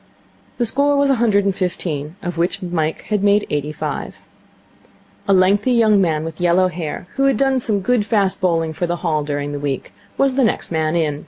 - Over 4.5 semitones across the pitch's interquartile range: Yes, average, 5.2 semitones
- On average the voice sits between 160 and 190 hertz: Yes, medium, 185 Hz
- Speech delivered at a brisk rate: Yes, fast, 210 wpm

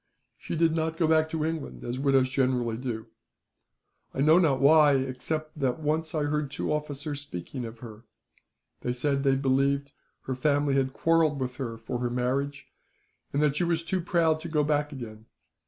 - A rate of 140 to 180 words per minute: No, average, 190 wpm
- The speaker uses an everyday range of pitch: Yes, average, 3.3 semitones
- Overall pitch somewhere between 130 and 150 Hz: Yes, medium, 140 Hz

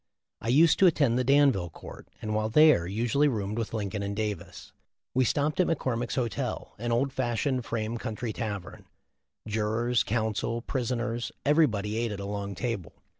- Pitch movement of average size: Yes, average, 3.4 semitones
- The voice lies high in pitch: No, low, 115 Hz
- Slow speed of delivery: No, average, 170 wpm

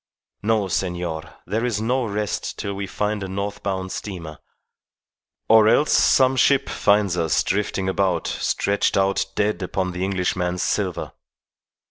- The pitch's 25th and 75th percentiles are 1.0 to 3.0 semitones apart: Yes, narrow, 2.5 semitones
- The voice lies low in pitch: Yes, low, 100 Hz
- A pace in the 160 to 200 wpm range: No, average, 140 wpm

